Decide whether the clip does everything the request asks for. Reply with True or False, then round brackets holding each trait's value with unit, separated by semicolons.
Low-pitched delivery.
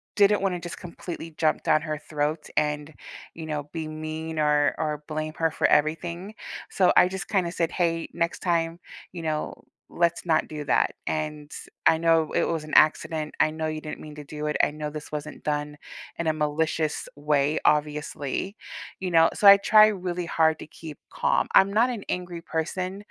False (160 Hz)